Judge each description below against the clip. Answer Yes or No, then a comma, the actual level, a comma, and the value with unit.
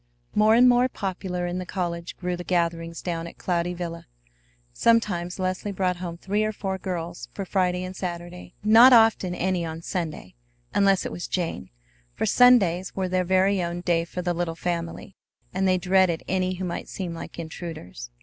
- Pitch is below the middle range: No, medium, 180 Hz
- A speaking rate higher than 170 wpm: Yes, average, 180 wpm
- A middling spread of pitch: No, narrow, 1.9 semitones